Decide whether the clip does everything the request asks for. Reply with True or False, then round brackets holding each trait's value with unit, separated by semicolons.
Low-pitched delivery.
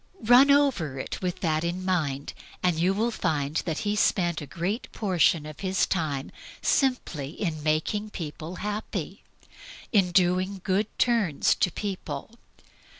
False (180 Hz)